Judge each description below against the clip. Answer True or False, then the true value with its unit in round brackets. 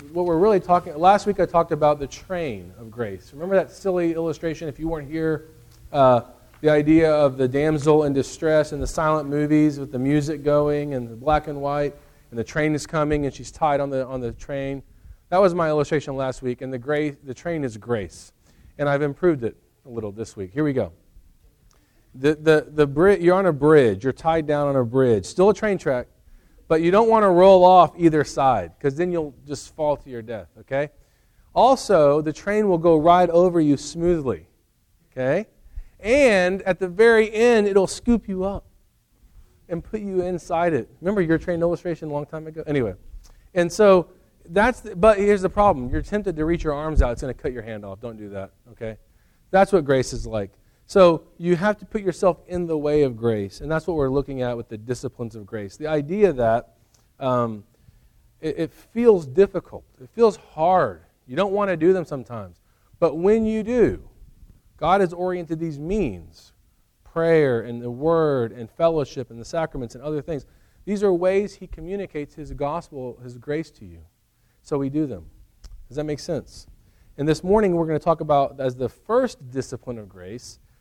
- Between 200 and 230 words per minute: True (205 wpm)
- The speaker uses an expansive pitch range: True (5.9 semitones)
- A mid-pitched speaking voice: True (150 Hz)